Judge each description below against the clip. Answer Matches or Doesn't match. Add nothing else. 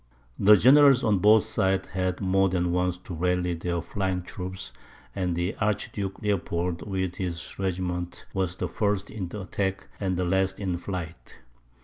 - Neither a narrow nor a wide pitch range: Doesn't match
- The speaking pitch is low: Matches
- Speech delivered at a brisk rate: Doesn't match